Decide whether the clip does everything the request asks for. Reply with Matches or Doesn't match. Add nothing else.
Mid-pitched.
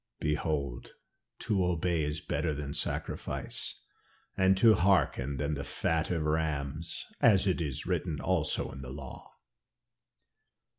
Doesn't match